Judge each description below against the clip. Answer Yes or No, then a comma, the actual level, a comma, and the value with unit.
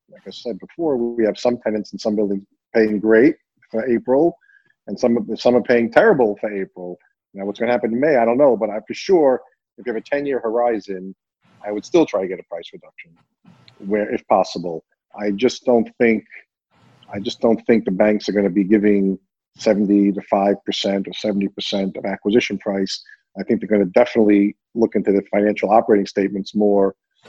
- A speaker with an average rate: No, fast, 210 wpm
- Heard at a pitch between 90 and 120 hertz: Yes, low, 105 Hz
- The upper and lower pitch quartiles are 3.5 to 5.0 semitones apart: No, average, 2.7 semitones